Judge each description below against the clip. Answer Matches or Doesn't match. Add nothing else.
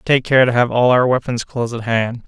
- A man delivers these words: Matches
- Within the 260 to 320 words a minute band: Matches